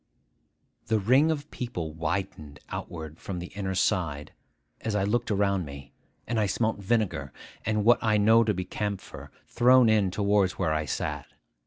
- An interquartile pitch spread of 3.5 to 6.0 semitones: Yes, average, 4.2 semitones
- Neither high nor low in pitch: No, low, 100 Hz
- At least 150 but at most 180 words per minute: Yes, average, 165 wpm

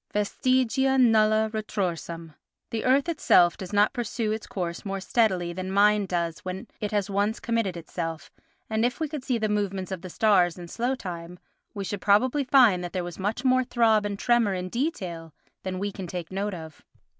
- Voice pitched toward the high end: Yes, high, 205 Hz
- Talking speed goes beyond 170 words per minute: Yes, average, 190 wpm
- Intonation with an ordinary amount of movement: Yes, average, 4.1 semitones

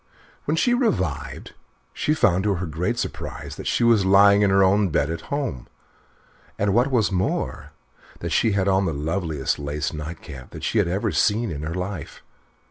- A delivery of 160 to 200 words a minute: Yes, average, 190 wpm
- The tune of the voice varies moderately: Yes, average, 4.8 semitones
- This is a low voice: Yes, very low, 95 Hz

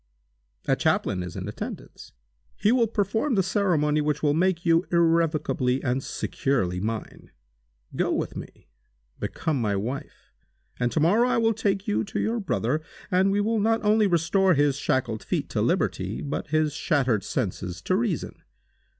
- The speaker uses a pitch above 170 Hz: No, medium, 165 Hz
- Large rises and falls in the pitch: Yes, wide, 7.0 semitones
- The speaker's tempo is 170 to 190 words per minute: No, average, 160 wpm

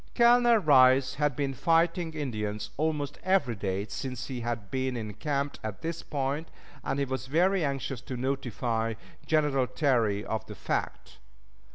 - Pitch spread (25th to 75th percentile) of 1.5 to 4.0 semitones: No, average, 4.5 semitones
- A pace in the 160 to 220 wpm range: No, average, 150 wpm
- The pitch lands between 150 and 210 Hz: No, low, 135 Hz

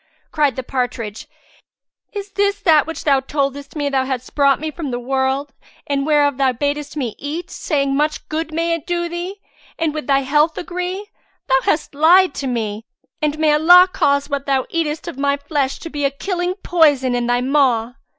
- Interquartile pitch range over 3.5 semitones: No, average, 3.2 semitones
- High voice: Yes, very high, 290 Hz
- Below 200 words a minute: Yes, average, 190 wpm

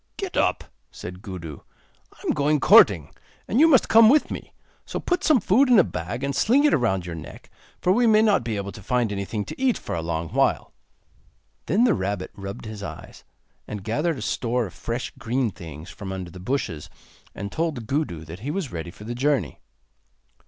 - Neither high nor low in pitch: No, low, 115 Hz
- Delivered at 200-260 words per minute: Yes, fast, 205 wpm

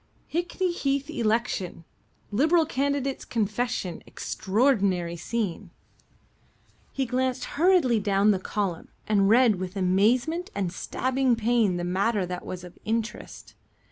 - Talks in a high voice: Yes, high, 225 Hz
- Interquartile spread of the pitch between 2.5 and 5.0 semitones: No, wide, 5.4 semitones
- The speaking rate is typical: No, slow, 115 wpm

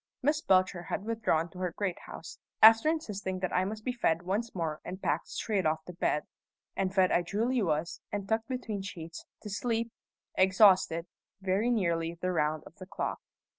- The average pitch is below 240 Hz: Yes, high, 190 Hz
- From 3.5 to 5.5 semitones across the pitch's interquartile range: Yes, average, 4.3 semitones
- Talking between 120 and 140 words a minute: No, average, 185 wpm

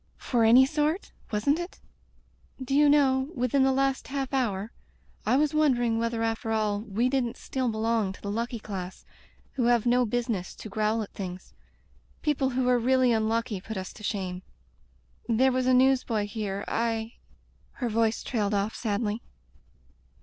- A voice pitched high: Yes, high, 230 Hz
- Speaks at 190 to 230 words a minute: No, average, 180 wpm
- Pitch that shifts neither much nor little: Yes, average, 3.5 semitones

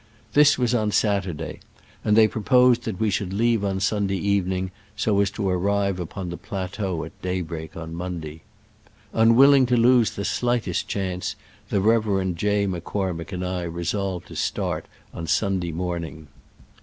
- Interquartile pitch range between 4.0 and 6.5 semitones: No, average, 3.3 semitones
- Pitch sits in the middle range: No, very low, 95 Hz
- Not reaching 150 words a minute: No, average, 160 wpm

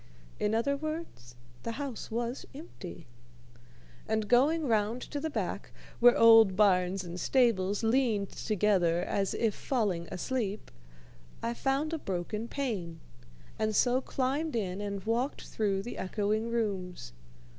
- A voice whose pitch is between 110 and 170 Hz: No, high, 220 Hz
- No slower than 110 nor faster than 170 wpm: Yes, slow, 135 wpm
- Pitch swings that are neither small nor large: Yes, average, 4.6 semitones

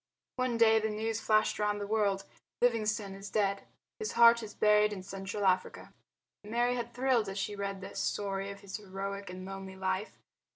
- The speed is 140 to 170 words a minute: No, average, 180 wpm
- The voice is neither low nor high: No, high, 205 Hz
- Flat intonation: Yes, narrow, 2.2 semitones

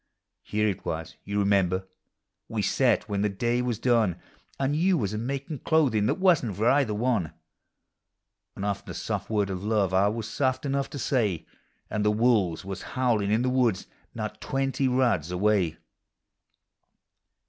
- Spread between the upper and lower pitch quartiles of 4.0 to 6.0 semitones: Yes, average, 4.4 semitones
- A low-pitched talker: Yes, low, 110 Hz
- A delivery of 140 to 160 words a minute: No, average, 170 wpm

